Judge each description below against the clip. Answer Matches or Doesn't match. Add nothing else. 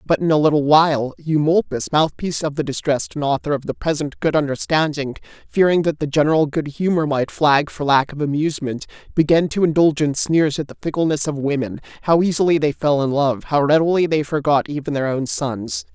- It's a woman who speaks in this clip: Doesn't match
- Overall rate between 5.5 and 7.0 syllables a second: Matches